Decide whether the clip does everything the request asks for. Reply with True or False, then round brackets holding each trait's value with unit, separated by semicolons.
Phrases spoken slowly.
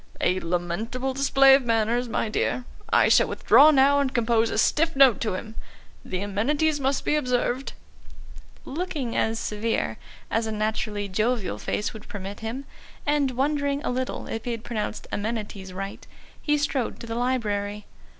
False (160 wpm)